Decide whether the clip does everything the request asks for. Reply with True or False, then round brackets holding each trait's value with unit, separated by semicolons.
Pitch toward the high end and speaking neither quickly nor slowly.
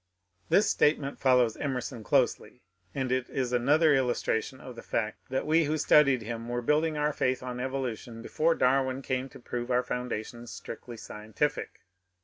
False (130 Hz; 165 wpm)